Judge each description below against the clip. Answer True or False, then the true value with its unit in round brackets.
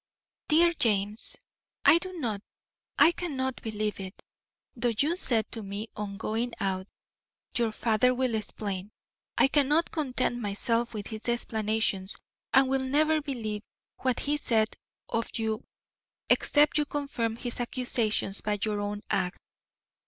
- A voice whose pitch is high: True (230 Hz)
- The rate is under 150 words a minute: True (135 wpm)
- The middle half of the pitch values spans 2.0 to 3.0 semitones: False (4.1 semitones)